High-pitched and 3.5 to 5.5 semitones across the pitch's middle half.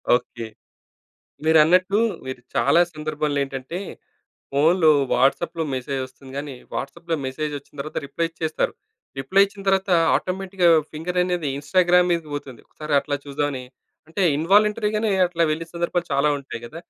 No: medium, 160 Hz; average, 4.1 semitones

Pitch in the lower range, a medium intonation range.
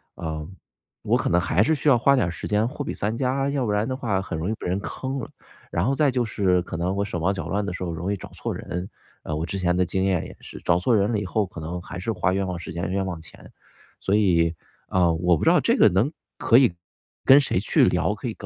Yes: very low, 95 Hz; average, 4.4 semitones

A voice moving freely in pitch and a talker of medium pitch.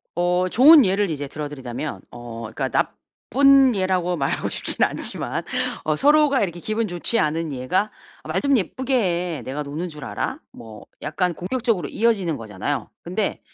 Yes: wide, 6.9 semitones; medium, 175 Hz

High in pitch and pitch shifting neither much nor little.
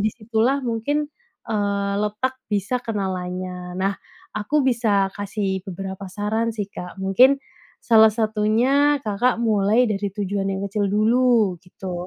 Yes: high, 210 Hz; average, 3.0 semitones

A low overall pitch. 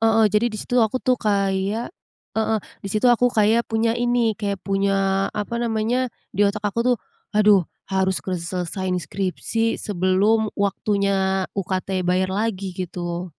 No: high, 200 Hz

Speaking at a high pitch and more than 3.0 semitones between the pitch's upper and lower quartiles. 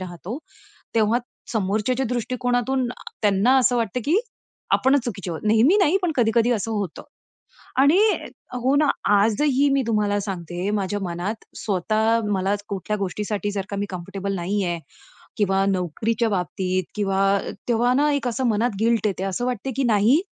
Yes: high, 215 Hz; average, 4.1 semitones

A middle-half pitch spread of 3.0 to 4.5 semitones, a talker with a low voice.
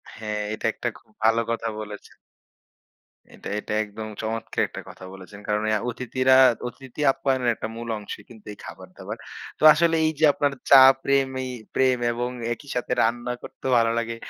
Yes: average, 3.3 semitones; low, 115 Hz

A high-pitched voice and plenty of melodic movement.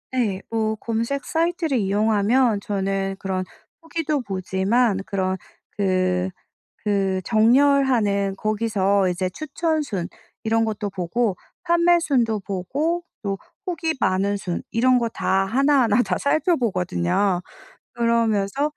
No: high, 215 Hz; average, 5.0 semitones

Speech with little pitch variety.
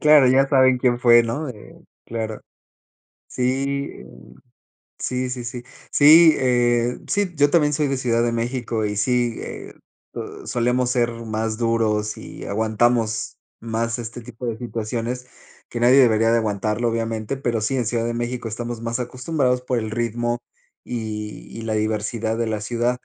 Yes: narrow, 2.0 semitones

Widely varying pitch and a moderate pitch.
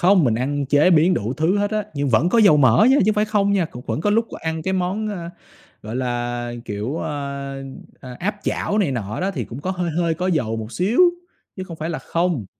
Yes: wide, 6.5 semitones; medium, 160 Hz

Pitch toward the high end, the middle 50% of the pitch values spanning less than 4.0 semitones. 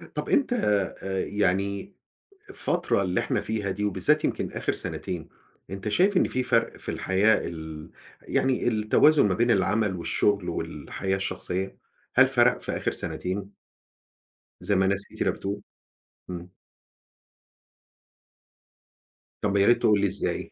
No: low, 100 Hz; average, 2.8 semitones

